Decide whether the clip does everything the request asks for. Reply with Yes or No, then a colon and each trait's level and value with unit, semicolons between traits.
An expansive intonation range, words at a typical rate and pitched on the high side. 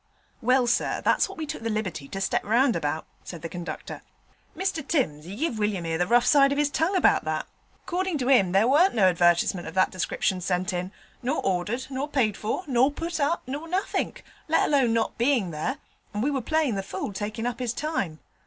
No: wide, 7.4 semitones; fast, 215 wpm; high, 240 Hz